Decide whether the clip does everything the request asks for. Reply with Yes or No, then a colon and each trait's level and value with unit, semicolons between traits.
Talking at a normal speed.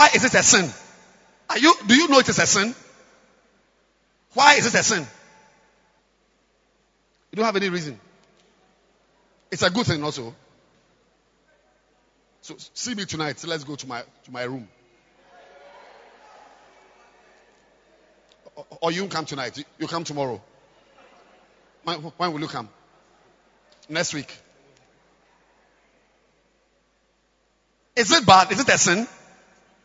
No: slow, 125 wpm